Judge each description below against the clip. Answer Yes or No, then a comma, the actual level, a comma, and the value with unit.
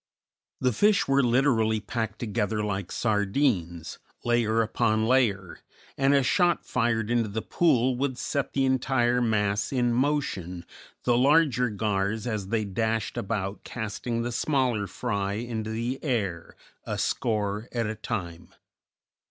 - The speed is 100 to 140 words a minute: Yes, slow, 135 wpm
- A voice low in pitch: Yes, low, 115 Hz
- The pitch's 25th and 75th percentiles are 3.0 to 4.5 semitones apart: Yes, average, 3.4 semitones